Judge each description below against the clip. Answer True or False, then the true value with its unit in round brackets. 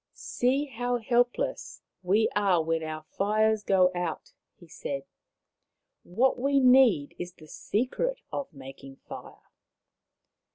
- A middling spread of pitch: False (7.3 semitones)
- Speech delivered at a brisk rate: False (140 wpm)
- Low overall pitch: False (205 Hz)